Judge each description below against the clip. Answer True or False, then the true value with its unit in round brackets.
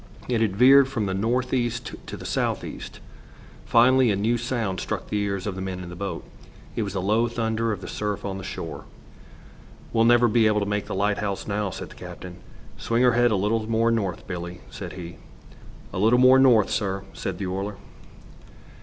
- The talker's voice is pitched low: True (105 Hz)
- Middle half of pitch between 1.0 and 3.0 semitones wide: False (3.4 semitones)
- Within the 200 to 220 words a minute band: True (205 wpm)